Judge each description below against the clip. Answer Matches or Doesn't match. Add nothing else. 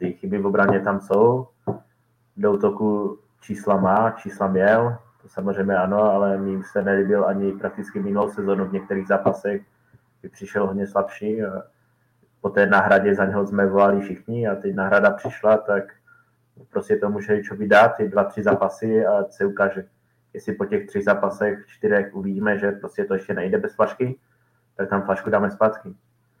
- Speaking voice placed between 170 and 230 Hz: Doesn't match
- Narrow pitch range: Matches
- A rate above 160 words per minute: Matches